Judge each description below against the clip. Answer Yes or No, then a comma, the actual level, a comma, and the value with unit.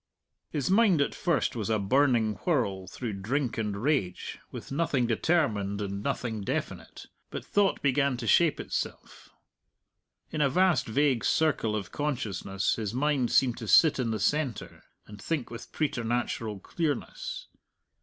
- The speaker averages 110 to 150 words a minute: Yes, average, 145 wpm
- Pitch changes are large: Yes, wide, 5.7 semitones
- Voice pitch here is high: No, low, 125 Hz